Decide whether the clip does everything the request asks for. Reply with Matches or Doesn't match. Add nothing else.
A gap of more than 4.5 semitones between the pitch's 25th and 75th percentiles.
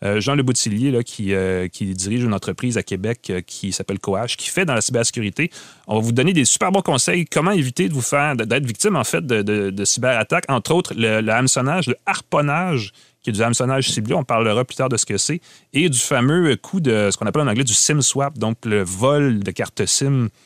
Matches